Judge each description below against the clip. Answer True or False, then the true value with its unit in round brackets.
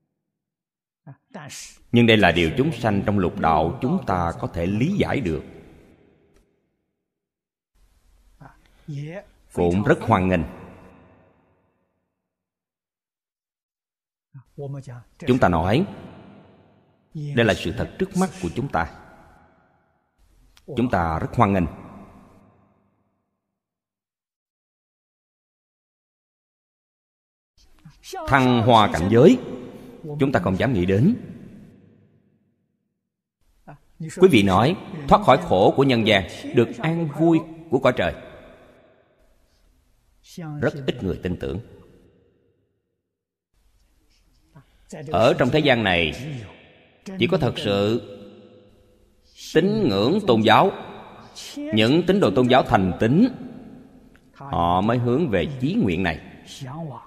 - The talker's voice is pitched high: False (100 Hz)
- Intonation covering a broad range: True (8.1 semitones)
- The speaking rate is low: True (100 wpm)